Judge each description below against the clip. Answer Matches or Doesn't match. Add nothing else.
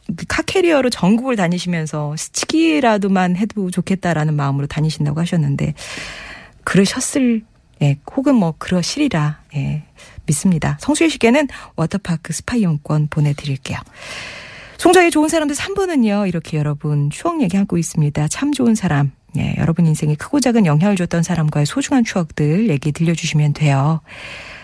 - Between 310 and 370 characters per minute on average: Matches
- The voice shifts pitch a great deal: Matches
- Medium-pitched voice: Matches